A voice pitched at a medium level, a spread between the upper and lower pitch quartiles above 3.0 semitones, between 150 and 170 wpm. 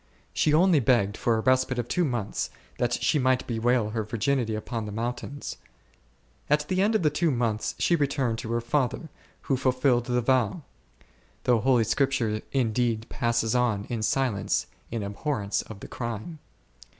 No: low, 120 Hz; average, 3.4 semitones; average, 165 wpm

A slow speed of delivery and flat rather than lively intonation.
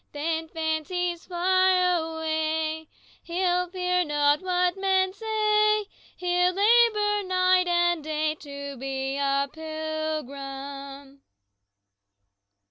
No: slow, 90 wpm; average, 3.4 semitones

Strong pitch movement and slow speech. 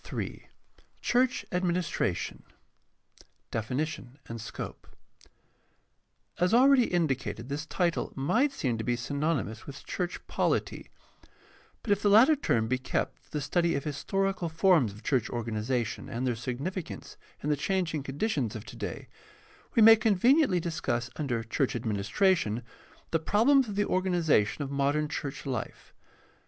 No: wide, 7.4 semitones; average, 145 wpm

